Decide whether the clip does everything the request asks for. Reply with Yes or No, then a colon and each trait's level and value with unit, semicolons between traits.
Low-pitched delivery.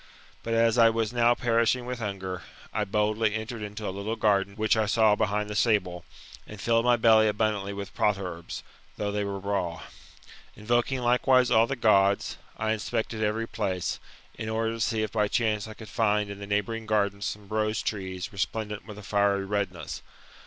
Yes: low, 105 Hz